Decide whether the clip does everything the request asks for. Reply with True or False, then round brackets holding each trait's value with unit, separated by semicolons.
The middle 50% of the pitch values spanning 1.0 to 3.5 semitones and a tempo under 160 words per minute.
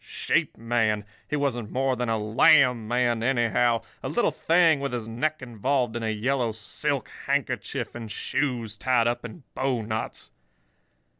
True (3.0 semitones; 140 wpm)